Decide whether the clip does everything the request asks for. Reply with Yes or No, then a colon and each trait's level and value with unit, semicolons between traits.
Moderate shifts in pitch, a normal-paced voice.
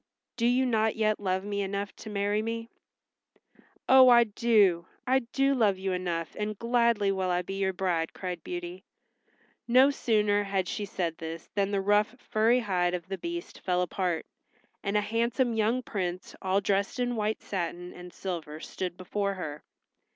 Yes: average, 3.9 semitones; average, 175 wpm